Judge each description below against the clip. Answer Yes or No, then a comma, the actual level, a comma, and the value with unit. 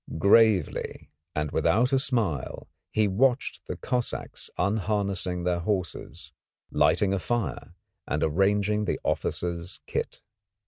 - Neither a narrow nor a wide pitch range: Yes, average, 3.7 semitones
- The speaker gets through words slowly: Yes, slow, 110 wpm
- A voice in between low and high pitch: No, low, 100 Hz